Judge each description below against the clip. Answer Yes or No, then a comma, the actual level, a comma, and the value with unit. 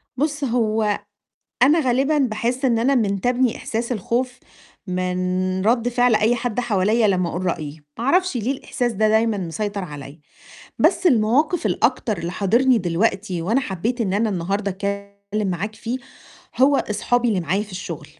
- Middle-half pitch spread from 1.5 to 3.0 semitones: No, average, 4.4 semitones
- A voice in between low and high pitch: No, high, 215 Hz